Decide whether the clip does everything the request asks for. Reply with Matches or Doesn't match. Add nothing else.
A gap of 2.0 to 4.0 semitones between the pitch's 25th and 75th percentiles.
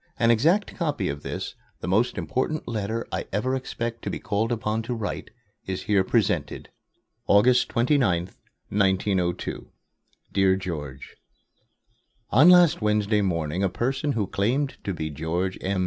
Doesn't match